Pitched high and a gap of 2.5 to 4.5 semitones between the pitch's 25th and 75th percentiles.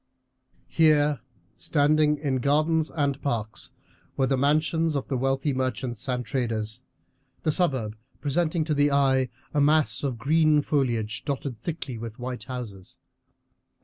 No: medium, 140 Hz; average, 3.3 semitones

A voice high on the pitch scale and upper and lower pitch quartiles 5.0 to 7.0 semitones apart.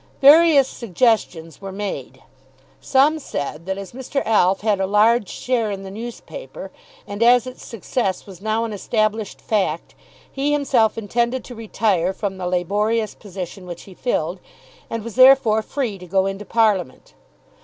No: high, 215 Hz; average, 3.8 semitones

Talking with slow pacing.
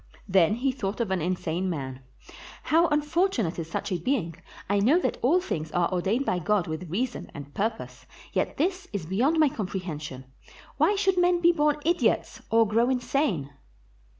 No: average, 175 wpm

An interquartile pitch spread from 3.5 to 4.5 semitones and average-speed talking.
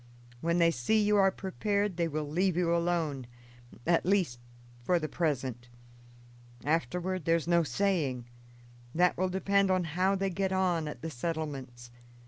Yes: average, 3.9 semitones; average, 150 wpm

